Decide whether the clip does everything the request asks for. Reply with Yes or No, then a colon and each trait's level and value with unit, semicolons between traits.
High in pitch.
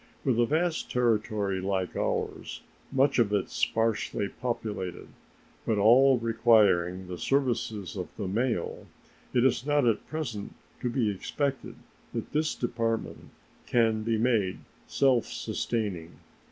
No: low, 115 Hz